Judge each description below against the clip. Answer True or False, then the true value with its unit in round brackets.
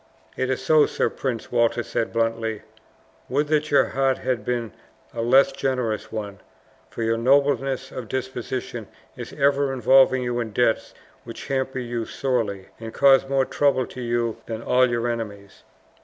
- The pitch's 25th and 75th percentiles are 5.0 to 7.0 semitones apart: False (2.7 semitones)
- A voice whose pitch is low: True (125 Hz)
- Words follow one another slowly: False (160 wpm)